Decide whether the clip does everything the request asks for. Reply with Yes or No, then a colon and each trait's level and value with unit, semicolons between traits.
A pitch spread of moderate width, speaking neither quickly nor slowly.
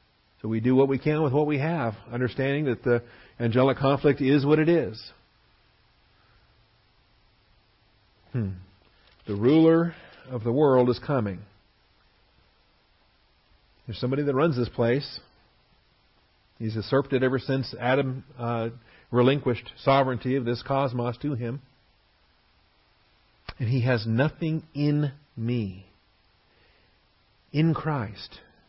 No: average, 3.8 semitones; slow, 115 wpm